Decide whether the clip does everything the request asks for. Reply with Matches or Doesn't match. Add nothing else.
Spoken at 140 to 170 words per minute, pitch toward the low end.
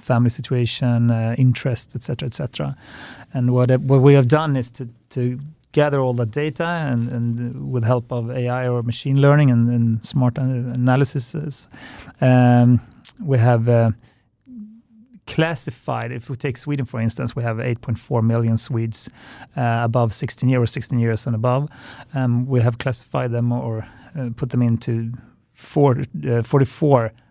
Matches